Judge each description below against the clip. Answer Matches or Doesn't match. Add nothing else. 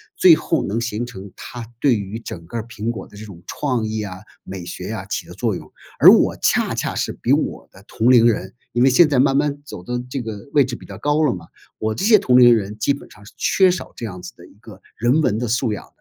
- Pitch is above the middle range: Doesn't match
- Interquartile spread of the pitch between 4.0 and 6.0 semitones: Matches